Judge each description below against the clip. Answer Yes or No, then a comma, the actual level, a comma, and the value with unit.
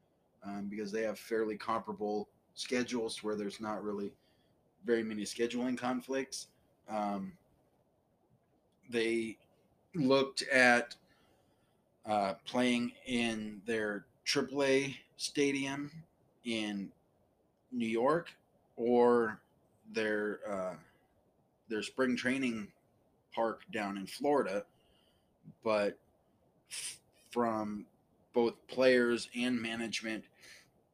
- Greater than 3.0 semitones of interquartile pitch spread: No, average, 2.7 semitones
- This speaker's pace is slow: Yes, slow, 85 wpm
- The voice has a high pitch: No, low, 115 Hz